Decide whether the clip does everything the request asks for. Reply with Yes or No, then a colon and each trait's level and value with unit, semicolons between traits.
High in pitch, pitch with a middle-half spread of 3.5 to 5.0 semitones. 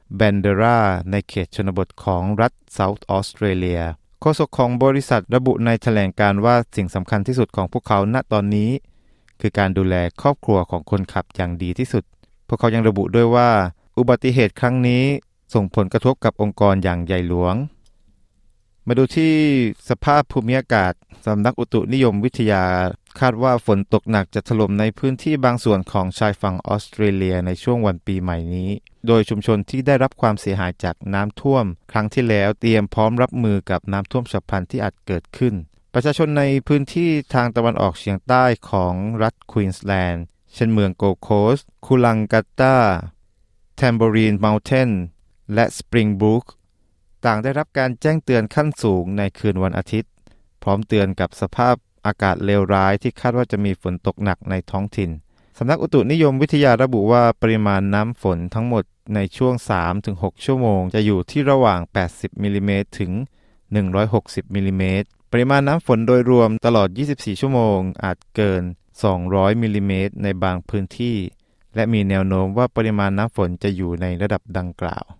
No: low, 105 Hz; average, 4.0 semitones